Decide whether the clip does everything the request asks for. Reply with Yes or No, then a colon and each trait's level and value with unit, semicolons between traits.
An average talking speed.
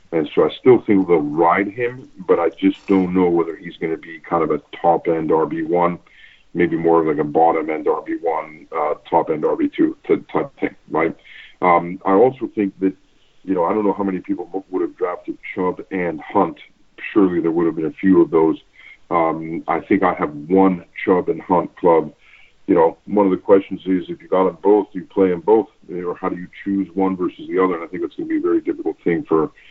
No: fast, 235 wpm